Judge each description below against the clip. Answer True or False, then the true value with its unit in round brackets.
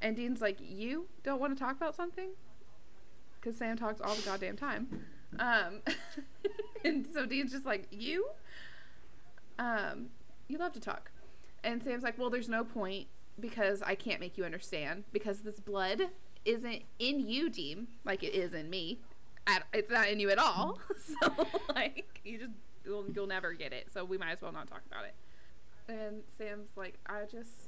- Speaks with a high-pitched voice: True (225 Hz)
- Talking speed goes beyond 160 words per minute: True (180 wpm)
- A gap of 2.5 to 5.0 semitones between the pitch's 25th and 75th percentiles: False (5.5 semitones)